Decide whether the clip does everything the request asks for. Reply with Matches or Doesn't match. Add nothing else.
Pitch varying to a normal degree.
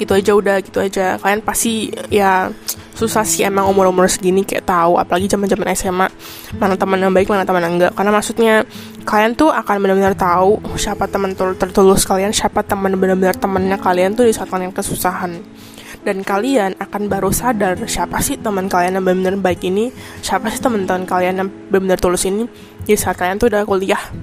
Doesn't match